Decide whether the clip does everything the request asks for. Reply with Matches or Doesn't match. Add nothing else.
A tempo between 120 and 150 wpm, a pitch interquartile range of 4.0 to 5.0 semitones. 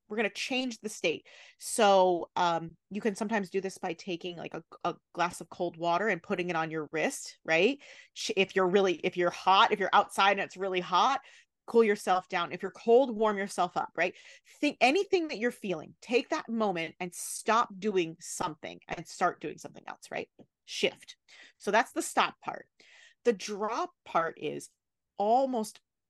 Doesn't match